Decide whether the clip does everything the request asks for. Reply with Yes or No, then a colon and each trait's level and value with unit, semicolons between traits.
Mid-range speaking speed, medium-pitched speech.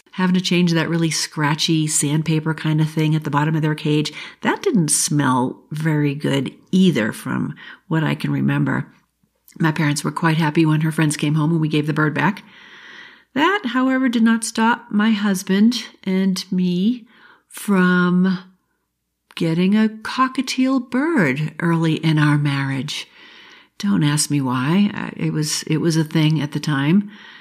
Yes: average, 160 wpm; medium, 165 Hz